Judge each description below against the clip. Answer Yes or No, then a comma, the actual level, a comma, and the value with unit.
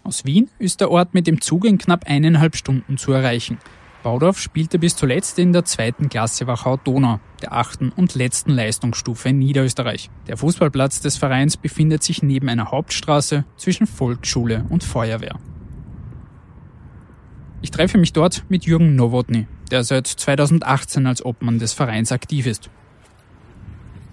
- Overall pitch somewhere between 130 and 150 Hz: Yes, low, 135 Hz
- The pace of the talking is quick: No, average, 145 wpm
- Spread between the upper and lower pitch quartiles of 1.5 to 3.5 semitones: No, average, 5.3 semitones